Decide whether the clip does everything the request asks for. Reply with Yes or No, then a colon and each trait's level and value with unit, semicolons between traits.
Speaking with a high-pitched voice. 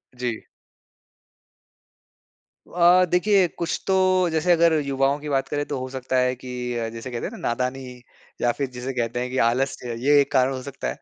No: low, 130 Hz